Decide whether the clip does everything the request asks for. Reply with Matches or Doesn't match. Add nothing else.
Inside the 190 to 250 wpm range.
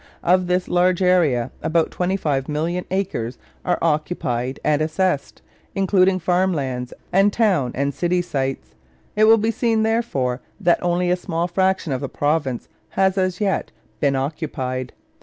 Doesn't match